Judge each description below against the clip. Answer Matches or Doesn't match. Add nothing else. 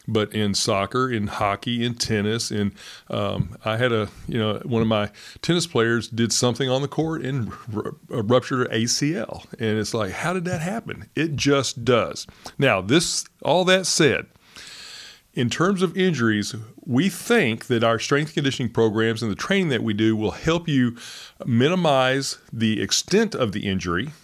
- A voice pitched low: Matches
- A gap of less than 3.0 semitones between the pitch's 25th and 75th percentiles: Doesn't match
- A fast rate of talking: Doesn't match